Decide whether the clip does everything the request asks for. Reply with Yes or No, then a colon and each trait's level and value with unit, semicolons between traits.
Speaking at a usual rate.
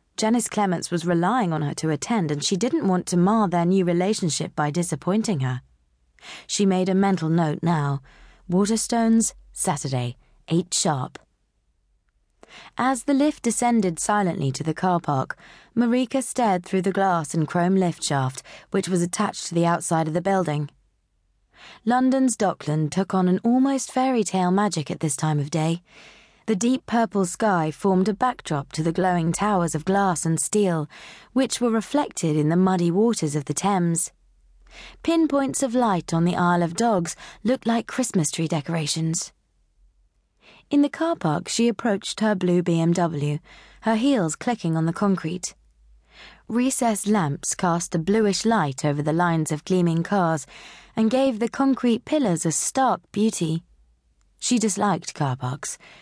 Yes: average, 160 wpm